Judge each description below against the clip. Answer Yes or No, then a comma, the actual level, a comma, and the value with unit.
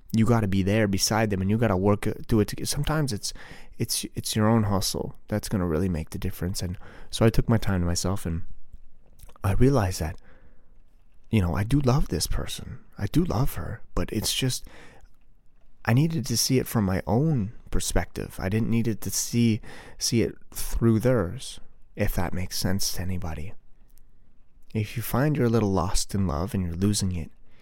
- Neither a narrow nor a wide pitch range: Yes, average, 3.9 semitones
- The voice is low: Yes, low, 105 Hz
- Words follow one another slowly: No, average, 200 wpm